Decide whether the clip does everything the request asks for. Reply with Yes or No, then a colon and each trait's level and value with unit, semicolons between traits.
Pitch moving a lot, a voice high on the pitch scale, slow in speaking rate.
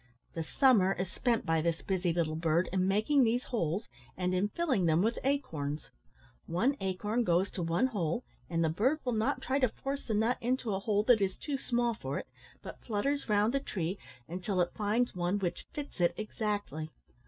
No: wide, 5.7 semitones; high, 205 Hz; average, 200 wpm